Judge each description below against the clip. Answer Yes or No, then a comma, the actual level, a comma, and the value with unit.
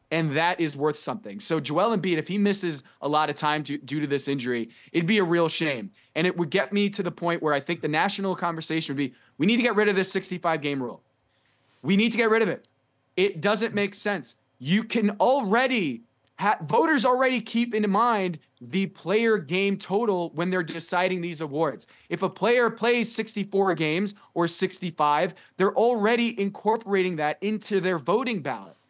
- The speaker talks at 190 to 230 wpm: Yes, average, 200 wpm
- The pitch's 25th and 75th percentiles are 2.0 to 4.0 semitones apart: No, average, 4.8 semitones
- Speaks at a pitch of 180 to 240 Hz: Yes, medium, 185 Hz